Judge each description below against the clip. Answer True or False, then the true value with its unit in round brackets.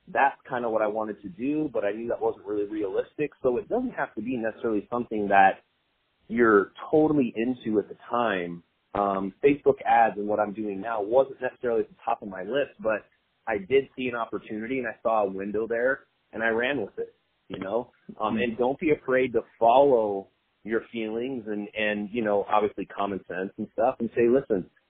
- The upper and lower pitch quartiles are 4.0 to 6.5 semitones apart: True (4.5 semitones)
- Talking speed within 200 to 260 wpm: True (205 wpm)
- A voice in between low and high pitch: False (115 Hz)